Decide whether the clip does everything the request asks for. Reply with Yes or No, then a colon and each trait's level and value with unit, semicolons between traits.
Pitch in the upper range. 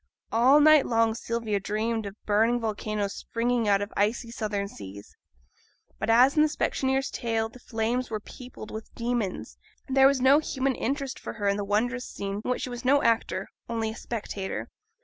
Yes: high, 230 Hz